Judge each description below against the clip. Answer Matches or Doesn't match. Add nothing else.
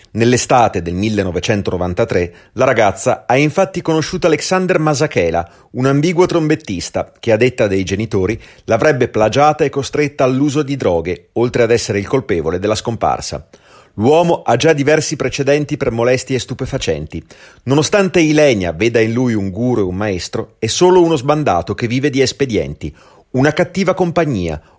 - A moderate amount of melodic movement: Doesn't match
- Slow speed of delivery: Doesn't match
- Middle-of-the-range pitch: Doesn't match